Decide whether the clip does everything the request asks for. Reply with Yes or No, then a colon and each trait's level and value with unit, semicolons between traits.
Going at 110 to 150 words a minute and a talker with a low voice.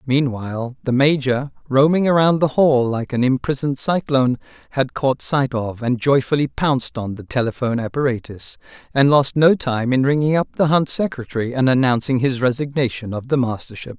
No: average, 165 wpm; low, 130 Hz